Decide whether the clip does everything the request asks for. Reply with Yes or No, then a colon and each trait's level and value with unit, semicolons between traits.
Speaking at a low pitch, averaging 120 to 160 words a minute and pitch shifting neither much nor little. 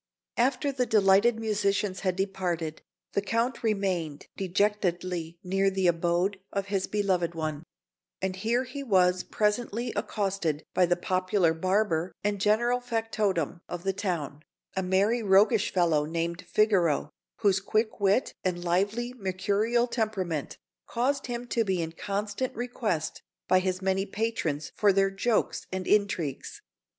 No: high, 195 Hz; average, 140 wpm; average, 3.4 semitones